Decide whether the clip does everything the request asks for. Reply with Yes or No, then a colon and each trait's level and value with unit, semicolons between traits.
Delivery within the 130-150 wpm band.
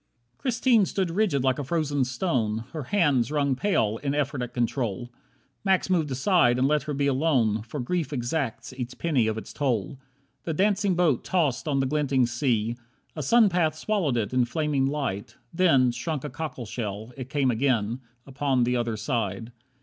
No: average, 180 wpm